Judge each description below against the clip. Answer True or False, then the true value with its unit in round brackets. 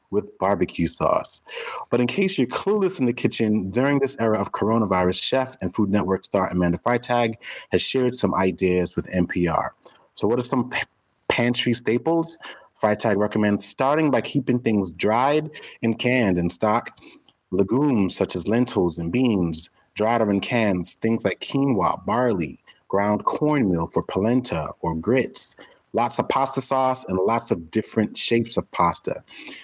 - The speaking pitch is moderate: False (115 Hz)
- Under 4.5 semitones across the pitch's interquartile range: False (4.9 semitones)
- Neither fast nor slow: True (160 wpm)